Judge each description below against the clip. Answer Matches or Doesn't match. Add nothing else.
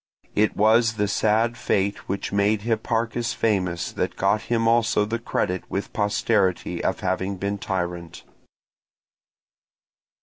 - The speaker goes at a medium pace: Doesn't match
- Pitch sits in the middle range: Doesn't match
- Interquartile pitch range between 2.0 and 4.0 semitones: Matches